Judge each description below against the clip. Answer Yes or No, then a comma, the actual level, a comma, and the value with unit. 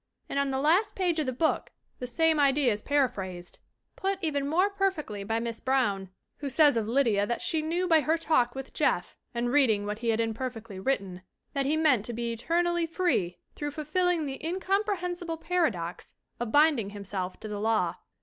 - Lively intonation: Yes, wide, 6.5 semitones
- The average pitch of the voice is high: Yes, very high, 270 Hz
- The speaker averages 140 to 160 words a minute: No, average, 190 wpm